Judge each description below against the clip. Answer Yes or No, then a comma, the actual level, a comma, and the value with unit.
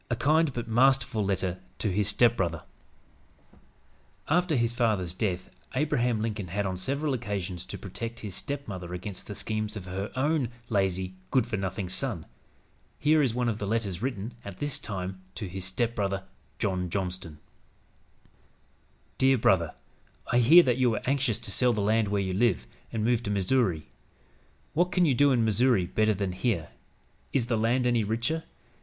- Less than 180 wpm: Yes, average, 170 wpm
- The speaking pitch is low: Yes, low, 110 Hz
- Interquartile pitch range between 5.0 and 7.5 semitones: No, average, 4.5 semitones